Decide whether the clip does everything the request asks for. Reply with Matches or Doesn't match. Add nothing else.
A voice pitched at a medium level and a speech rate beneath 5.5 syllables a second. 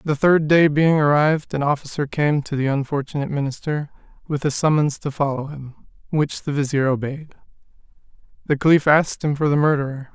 Doesn't match